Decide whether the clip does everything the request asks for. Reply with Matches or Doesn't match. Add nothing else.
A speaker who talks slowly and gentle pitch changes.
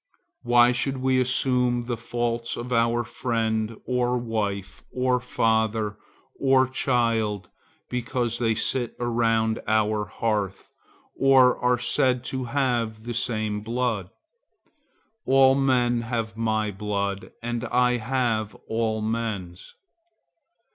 Matches